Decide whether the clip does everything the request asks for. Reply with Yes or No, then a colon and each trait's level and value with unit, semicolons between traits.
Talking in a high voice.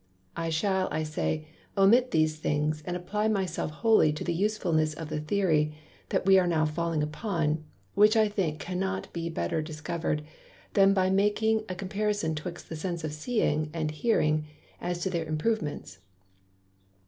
No: medium, 170 Hz